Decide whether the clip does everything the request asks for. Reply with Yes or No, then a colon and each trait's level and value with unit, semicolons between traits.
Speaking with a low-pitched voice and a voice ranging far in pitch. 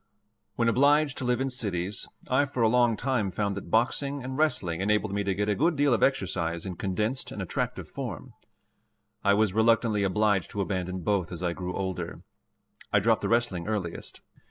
No: low, 105 Hz; average, 4.7 semitones